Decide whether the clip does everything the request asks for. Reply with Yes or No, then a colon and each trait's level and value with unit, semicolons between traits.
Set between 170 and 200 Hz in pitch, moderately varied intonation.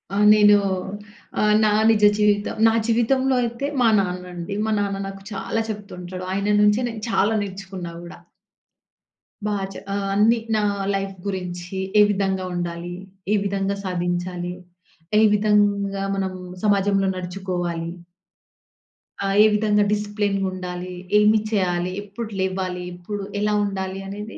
No: high, 195 Hz; narrow, 2.2 semitones